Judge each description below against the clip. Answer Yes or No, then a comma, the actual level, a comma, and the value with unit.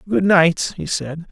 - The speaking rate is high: No, average, 185 wpm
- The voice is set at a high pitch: No, medium, 165 Hz